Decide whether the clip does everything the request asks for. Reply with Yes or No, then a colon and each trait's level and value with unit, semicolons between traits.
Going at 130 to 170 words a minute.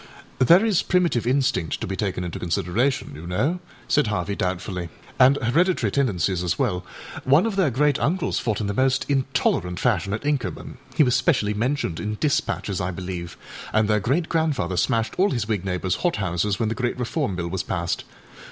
No: average, 185 wpm